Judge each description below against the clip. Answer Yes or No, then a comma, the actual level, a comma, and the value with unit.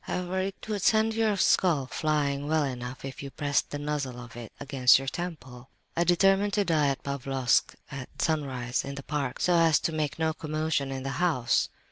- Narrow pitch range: No, average, 4.2 semitones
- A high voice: No, medium, 145 Hz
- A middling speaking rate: Yes, average, 190 wpm